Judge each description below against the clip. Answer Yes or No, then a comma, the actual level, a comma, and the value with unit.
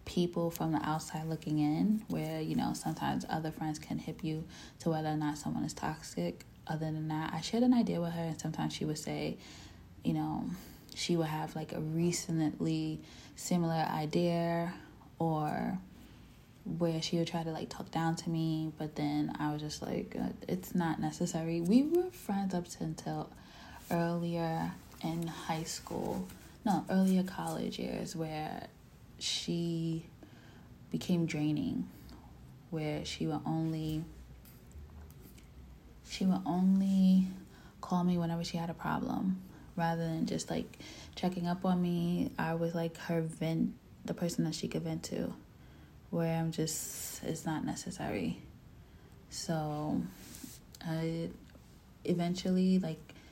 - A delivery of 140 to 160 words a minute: Yes, average, 145 wpm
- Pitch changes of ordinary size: No, narrow, 2.2 semitones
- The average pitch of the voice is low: No, medium, 165 Hz